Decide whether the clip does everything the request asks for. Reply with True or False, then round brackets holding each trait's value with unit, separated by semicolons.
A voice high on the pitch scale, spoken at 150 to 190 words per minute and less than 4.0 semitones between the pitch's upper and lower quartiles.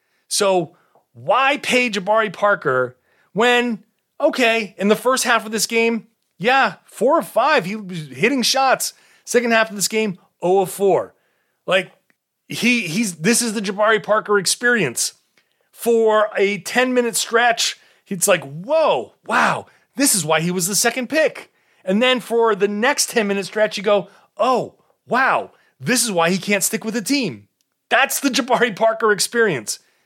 True (220 Hz; 165 wpm; 3.5 semitones)